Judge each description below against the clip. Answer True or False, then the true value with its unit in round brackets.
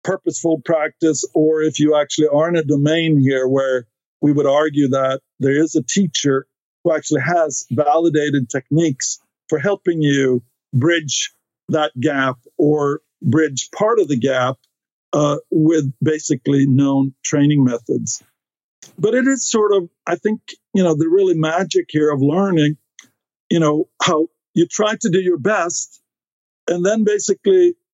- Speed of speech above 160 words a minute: False (150 wpm)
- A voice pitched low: False (155 Hz)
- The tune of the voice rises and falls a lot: False (3.6 semitones)